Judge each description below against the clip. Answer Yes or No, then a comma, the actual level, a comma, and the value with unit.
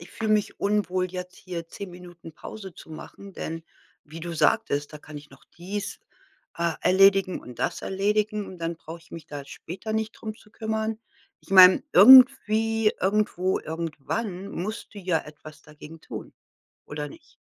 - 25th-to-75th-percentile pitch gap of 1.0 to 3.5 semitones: No, average, 4.4 semitones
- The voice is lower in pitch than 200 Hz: Yes, medium, 185 Hz